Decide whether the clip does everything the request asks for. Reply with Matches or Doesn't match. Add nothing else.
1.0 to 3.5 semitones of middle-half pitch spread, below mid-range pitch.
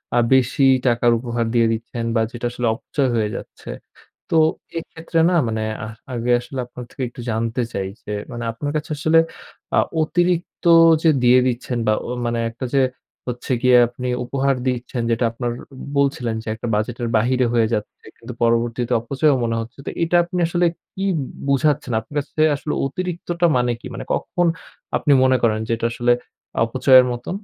Matches